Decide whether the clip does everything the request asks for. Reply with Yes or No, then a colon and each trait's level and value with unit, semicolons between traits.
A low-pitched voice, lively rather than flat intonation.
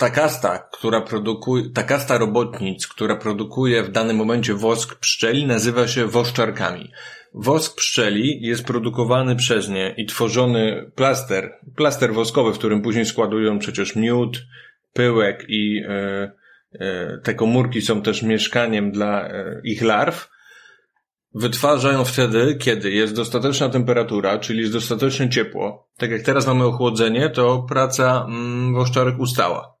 No: low, 120 Hz; narrow, 2.4 semitones